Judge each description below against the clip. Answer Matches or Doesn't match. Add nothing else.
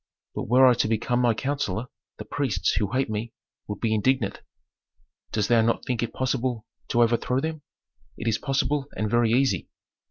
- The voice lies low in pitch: Matches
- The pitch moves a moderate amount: Matches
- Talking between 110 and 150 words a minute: Doesn't match